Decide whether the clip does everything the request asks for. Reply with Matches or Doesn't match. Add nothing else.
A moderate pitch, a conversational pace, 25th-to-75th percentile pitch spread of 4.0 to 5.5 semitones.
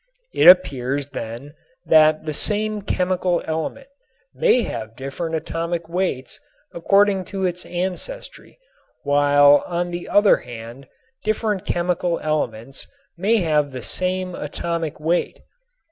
Doesn't match